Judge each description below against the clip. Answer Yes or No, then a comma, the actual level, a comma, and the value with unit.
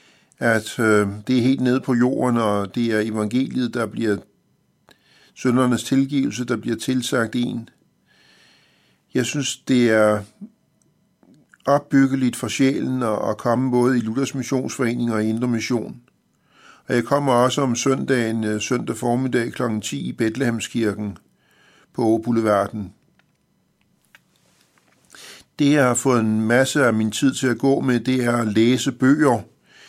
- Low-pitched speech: Yes, low, 120 Hz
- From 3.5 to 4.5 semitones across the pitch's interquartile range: No, average, 2.7 semitones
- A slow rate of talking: Yes, slow, 140 wpm